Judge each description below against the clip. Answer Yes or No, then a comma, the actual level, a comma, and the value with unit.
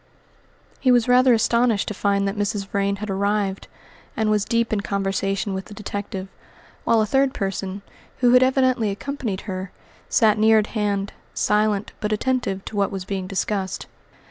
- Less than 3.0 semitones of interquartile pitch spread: Yes, narrow, 2.4 semitones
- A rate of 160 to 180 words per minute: Yes, average, 170 wpm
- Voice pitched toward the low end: No, high, 205 Hz